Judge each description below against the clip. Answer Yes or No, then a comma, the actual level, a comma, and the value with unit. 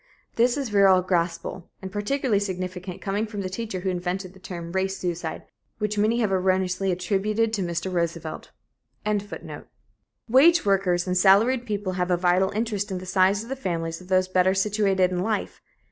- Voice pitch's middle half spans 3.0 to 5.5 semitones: No, narrow, 2.4 semitones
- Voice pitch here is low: No, high, 190 Hz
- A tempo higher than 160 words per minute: Yes, average, 175 wpm